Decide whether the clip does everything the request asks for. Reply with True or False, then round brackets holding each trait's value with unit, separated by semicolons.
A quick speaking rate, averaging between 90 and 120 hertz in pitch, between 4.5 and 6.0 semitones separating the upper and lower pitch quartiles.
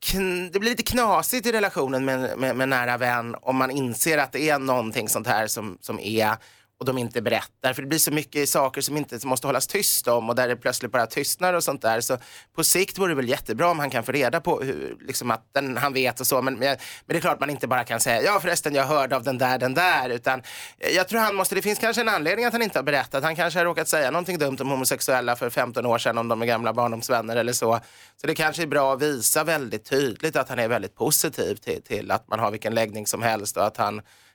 False (265 wpm; 135 Hz; 5.4 semitones)